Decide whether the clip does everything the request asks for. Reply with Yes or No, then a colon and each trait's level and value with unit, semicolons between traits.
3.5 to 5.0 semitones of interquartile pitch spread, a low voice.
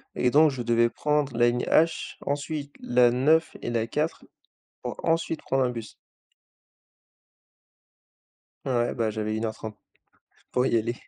Yes: average, 4.1 semitones; low, 125 Hz